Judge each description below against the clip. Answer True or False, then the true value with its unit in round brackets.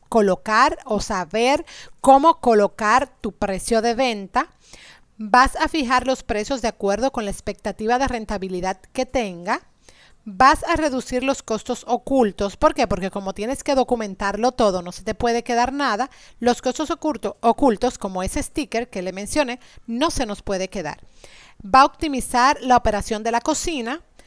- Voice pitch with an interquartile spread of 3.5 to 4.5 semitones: True (4.2 semitones)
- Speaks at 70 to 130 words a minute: False (165 wpm)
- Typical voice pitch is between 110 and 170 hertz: False (240 Hz)